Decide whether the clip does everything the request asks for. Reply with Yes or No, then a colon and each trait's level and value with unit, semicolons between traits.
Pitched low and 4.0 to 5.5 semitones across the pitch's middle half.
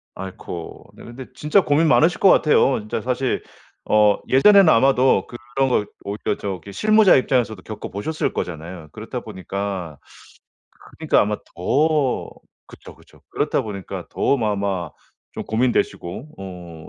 No: low, 110 Hz; wide, 6.2 semitones